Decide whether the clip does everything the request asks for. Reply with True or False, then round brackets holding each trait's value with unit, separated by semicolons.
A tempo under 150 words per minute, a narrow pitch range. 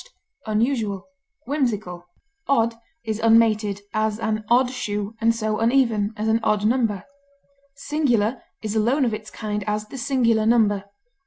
True (140 wpm; 2.1 semitones)